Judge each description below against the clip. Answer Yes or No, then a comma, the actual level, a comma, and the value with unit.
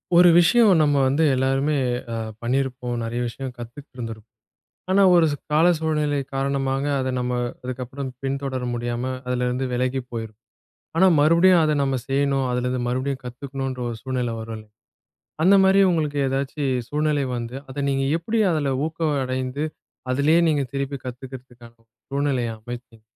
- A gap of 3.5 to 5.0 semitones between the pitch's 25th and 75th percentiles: No, average, 2.8 semitones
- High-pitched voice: No, low, 135 Hz